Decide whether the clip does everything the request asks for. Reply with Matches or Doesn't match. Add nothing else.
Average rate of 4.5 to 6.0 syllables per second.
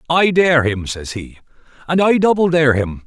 Matches